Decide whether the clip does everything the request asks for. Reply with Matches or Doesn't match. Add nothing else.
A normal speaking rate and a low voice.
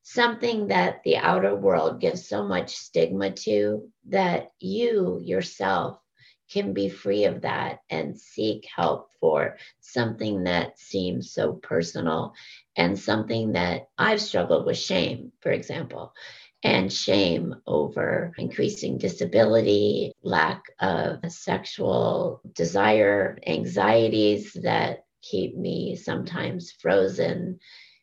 Doesn't match